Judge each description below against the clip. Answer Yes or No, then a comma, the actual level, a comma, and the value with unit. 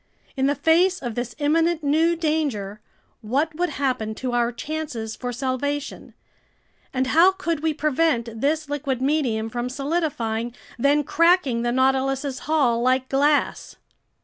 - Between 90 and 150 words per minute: Yes, average, 140 wpm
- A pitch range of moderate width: Yes, average, 4.2 semitones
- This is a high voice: Yes, very high, 275 Hz